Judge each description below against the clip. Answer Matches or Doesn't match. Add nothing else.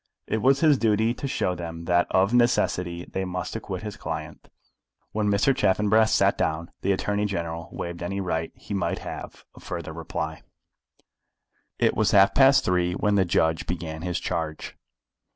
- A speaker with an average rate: Matches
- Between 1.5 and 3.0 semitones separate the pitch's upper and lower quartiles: Doesn't match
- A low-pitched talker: Matches